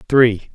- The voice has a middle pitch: No, low, 115 Hz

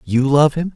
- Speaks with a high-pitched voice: No, medium, 145 Hz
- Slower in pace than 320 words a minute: Yes, fast, 240 wpm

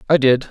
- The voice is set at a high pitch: No, low, 135 Hz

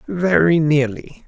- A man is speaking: Yes, male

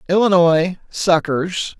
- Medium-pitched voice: Yes, medium, 175 Hz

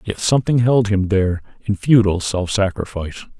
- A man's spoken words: Yes, male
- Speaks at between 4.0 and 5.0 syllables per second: No, 5.9 syllables/s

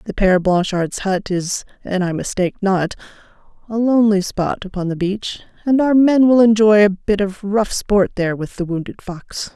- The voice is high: Yes, high, 200 Hz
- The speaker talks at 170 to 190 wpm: Yes, average, 175 wpm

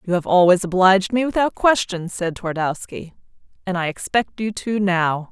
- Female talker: Yes, female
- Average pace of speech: Yes, average, 170 wpm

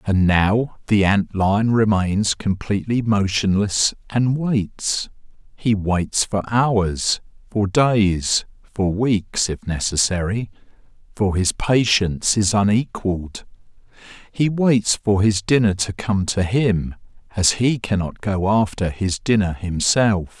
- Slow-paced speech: Yes, slow, 125 wpm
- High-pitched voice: No, low, 105 Hz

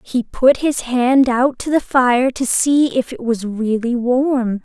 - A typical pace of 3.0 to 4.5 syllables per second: Yes, 3.5 syllables/s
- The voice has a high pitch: Yes, very high, 250 Hz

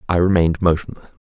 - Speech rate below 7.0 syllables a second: No, 7.4 syllables/s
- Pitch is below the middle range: Yes, very low, 85 Hz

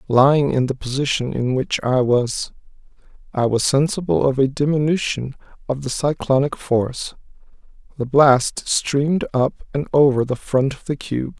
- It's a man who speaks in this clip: Yes, male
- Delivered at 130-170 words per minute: Yes, average, 155 wpm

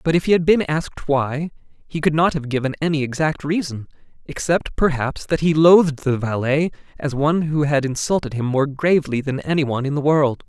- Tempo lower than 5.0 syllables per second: No, 5.5 syllables/s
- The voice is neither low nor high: Yes, medium, 150 Hz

